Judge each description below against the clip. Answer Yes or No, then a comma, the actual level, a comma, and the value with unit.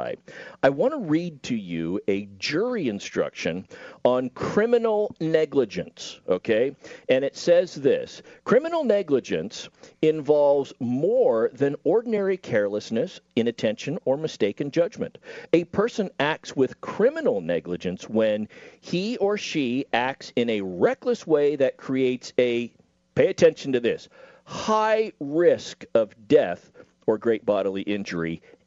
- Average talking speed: No, slow, 120 wpm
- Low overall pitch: No, medium, 150 Hz